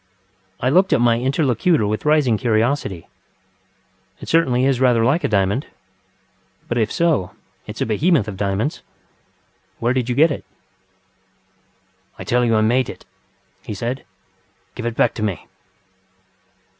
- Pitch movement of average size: Yes, average, 4.3 semitones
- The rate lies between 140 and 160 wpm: Yes, average, 150 wpm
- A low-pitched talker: Yes, low, 120 Hz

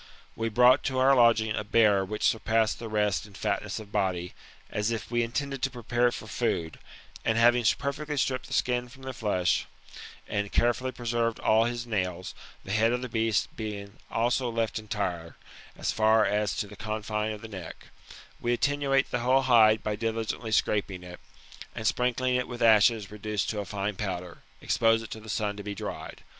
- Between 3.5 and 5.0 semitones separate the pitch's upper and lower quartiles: No, narrow, 2.6 semitones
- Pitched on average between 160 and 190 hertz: No, low, 110 Hz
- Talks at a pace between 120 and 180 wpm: No, average, 195 wpm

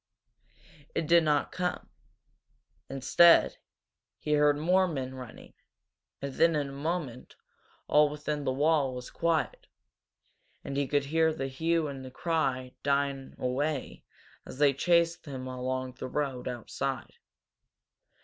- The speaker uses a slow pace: Yes, slow, 130 wpm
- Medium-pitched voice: Yes, medium, 145 Hz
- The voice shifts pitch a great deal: No, average, 3.4 semitones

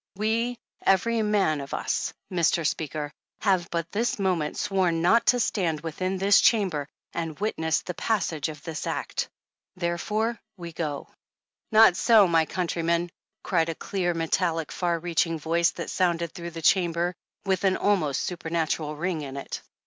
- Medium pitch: Yes, medium, 170 Hz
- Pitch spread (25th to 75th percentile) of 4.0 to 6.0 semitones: No, average, 3.0 semitones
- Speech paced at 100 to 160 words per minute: Yes, average, 155 wpm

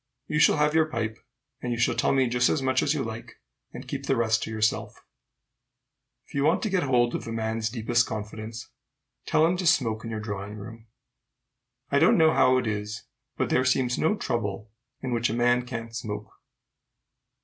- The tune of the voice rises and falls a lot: No, average, 3.0 semitones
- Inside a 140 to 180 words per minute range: No, average, 200 wpm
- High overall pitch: No, low, 120 Hz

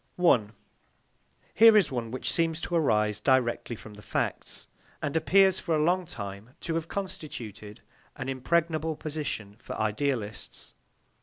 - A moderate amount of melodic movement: No, wide, 7.3 semitones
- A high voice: No, medium, 140 Hz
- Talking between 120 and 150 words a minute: Yes, average, 140 wpm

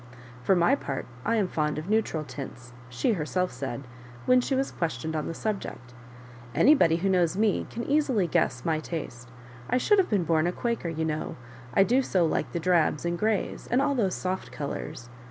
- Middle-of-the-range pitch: Yes, medium, 175 Hz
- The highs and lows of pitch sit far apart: Yes, wide, 6.3 semitones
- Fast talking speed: Yes, fast, 210 wpm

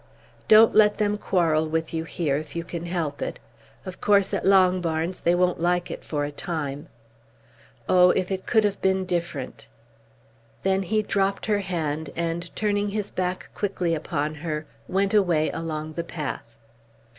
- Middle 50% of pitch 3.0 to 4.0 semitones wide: Yes, average, 3.4 semitones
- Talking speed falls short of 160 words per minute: No, average, 165 wpm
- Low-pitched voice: No, medium, 175 Hz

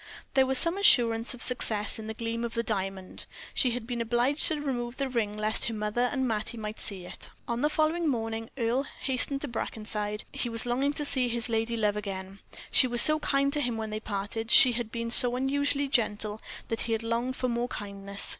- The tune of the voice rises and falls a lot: No, average, 3.1 semitones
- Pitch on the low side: No, high, 235 Hz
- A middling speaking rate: No, fast, 220 wpm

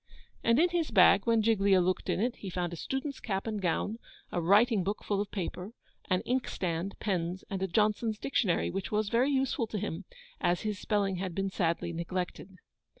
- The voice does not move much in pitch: No, average, 3.5 semitones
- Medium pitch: No, high, 200 Hz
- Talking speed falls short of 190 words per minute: No, average, 195 wpm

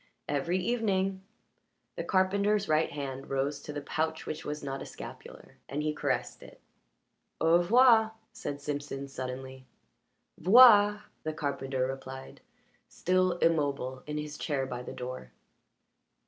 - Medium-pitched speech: Yes, medium, 150 Hz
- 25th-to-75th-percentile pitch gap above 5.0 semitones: Yes, wide, 5.6 semitones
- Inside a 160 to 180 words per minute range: No, slow, 135 wpm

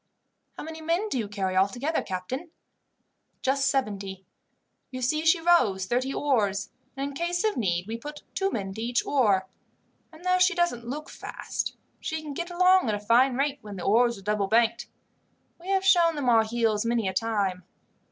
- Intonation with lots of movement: Yes, wide, 7.4 semitones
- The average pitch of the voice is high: Yes, high, 245 Hz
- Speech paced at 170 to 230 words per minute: Yes, average, 190 wpm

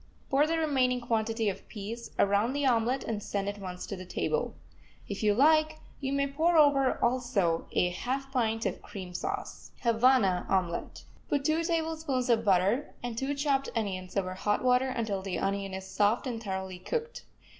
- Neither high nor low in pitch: No, high, 235 Hz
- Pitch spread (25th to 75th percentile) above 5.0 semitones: Yes, wide, 5.6 semitones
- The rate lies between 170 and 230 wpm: Yes, average, 175 wpm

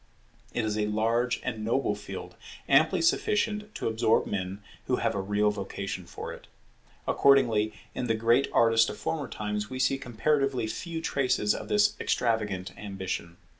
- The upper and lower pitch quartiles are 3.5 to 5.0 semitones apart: Yes, average, 4.4 semitones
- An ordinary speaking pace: Yes, average, 160 wpm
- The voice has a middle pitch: No, low, 115 Hz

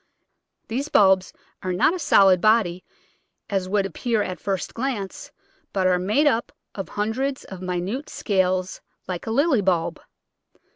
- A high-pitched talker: Yes, high, 195 Hz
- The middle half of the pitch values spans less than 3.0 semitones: No, average, 3.9 semitones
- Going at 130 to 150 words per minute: Yes, average, 145 wpm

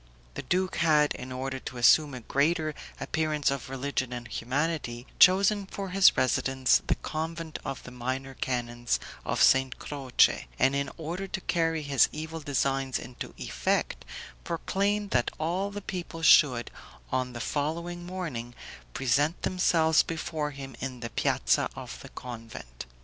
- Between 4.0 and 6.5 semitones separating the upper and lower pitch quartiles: Yes, average, 4.5 semitones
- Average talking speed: Yes, average, 150 wpm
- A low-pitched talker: No, medium, 145 Hz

